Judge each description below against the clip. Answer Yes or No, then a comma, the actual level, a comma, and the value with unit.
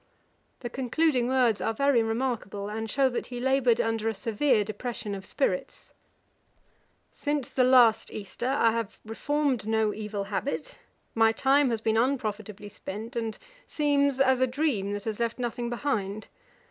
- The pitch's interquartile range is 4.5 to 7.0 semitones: No, average, 3.5 semitones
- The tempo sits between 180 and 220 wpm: No, average, 155 wpm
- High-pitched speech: Yes, high, 235 Hz